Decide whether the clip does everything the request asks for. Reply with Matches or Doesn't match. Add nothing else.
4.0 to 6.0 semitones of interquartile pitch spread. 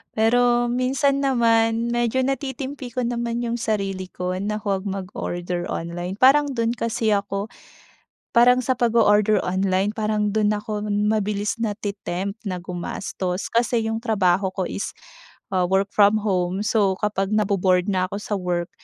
Doesn't match